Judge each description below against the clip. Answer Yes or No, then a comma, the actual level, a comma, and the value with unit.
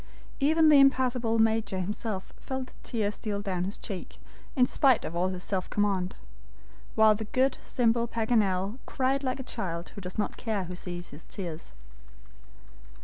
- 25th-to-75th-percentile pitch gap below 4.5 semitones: No, average, 5.1 semitones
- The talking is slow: No, average, 165 wpm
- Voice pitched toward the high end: Yes, high, 215 Hz